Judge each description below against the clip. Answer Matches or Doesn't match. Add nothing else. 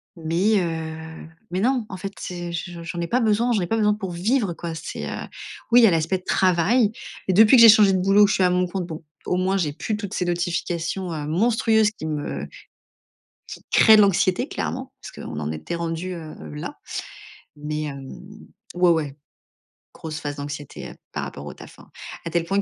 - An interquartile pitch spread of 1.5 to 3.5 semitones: Doesn't match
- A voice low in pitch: Doesn't match